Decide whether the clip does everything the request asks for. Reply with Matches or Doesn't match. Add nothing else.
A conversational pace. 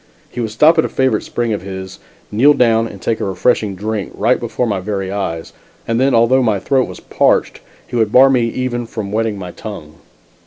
Doesn't match